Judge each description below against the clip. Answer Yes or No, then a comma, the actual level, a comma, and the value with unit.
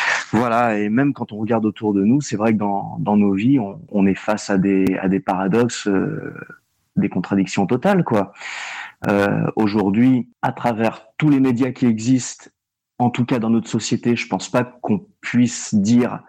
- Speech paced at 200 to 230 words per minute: No, average, 190 wpm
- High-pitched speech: No, low, 115 Hz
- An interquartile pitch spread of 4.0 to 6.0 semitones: No, average, 3.3 semitones